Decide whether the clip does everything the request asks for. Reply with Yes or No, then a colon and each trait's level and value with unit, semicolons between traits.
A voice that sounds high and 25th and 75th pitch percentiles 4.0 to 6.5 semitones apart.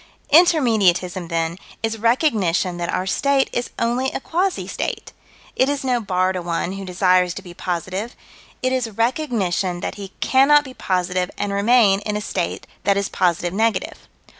Yes: high, 200 Hz; average, 5.3 semitones